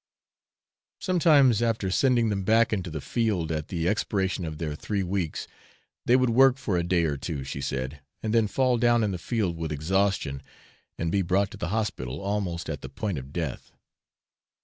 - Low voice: Yes, very low, 95 Hz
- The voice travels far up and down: Yes, wide, 5.7 semitones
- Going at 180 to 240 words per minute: Yes, average, 190 wpm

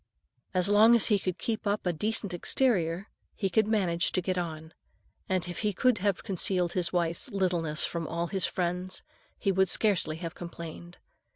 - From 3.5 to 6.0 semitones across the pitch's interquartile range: No, average, 2.9 semitones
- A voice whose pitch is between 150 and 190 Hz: Yes, medium, 185 Hz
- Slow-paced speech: No, average, 180 wpm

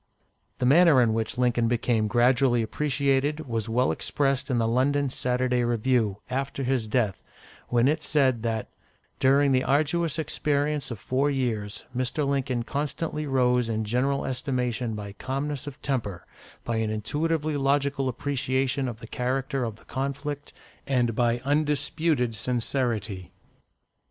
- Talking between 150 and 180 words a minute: No, average, 140 wpm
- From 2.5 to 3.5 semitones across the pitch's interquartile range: Yes, average, 3.1 semitones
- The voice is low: Yes, low, 130 Hz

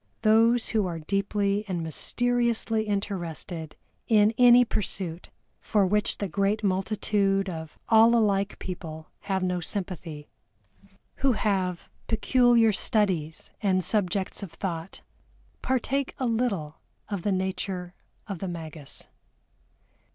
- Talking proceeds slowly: Yes, slow, 115 wpm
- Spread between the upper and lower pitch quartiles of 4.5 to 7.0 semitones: No, average, 3.6 semitones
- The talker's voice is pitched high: Yes, high, 195 Hz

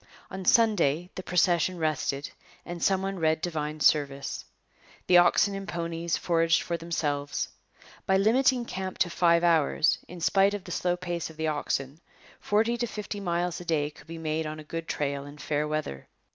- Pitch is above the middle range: No, medium, 170 Hz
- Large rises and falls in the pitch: No, average, 3.3 semitones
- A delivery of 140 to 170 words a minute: No, average, 180 wpm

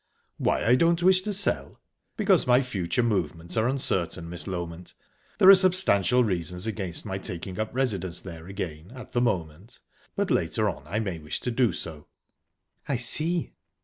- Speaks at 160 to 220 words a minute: Yes, average, 170 wpm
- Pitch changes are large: Yes, wide, 6.7 semitones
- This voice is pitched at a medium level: No, low, 105 Hz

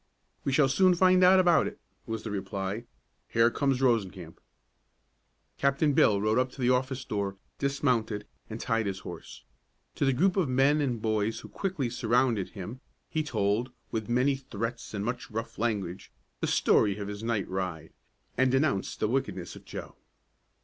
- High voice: No, low, 120 Hz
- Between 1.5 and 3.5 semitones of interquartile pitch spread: No, average, 4.7 semitones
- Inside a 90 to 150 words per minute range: No, average, 170 wpm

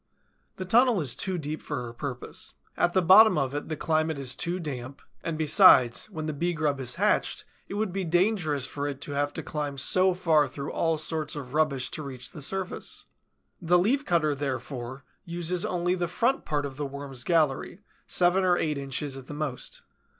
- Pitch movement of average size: Yes, average, 4.1 semitones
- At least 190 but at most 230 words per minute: Yes, average, 200 wpm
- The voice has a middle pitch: Yes, medium, 155 Hz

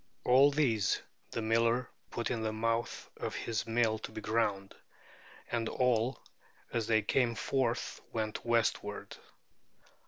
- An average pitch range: No, narrow, 1.5 semitones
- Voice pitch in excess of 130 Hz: No, low, 115 Hz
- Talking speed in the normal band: No, slow, 130 wpm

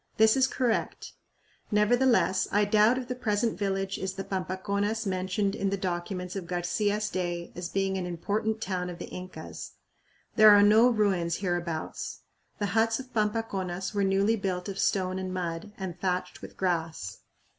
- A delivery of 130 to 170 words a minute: Yes, average, 165 wpm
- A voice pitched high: Yes, high, 195 Hz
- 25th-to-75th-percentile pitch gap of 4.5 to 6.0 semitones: No, average, 2.7 semitones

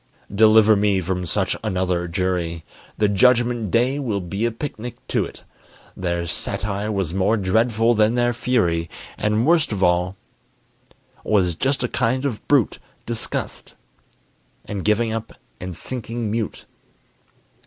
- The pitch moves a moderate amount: Yes, average, 4.1 semitones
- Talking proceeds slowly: Yes, slow, 130 wpm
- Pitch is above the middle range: No, low, 105 Hz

